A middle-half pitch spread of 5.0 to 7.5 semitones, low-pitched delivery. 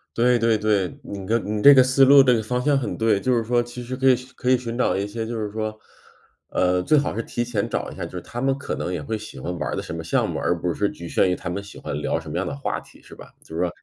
No: average, 3.9 semitones; low, 115 Hz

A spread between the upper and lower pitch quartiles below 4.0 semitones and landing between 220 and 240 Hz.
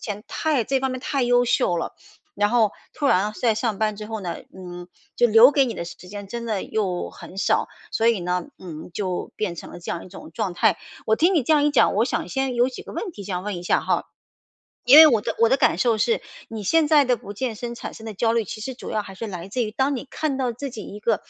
No: average, 4.3 semitones; high, 225 Hz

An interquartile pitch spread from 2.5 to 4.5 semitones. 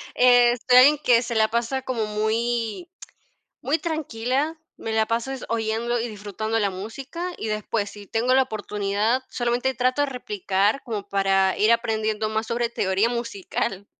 Yes: average, 2.8 semitones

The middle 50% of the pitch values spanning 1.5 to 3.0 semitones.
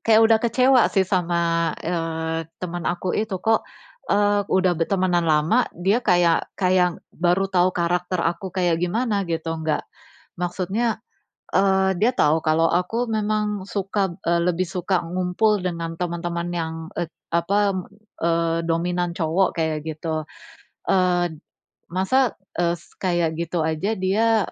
Yes: average, 2.7 semitones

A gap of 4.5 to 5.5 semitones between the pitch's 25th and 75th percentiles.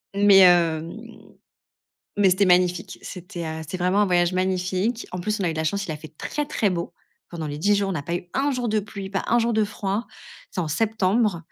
No: average, 3.0 semitones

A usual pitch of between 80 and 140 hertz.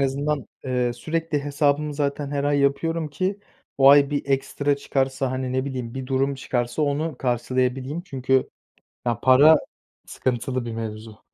Yes: low, 135 Hz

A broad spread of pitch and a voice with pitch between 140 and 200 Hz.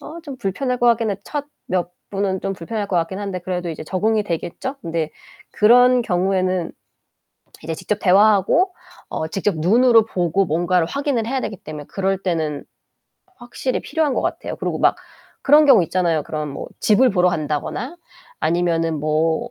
Yes: wide, 5.8 semitones; high, 190 Hz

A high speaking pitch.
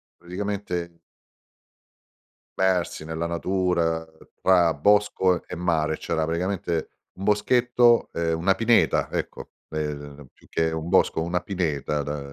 No: very low, 85 Hz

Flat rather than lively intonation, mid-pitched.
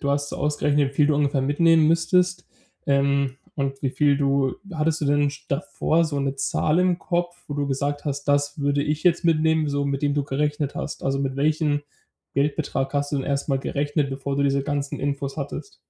Yes: narrow, 1.6 semitones; medium, 145 Hz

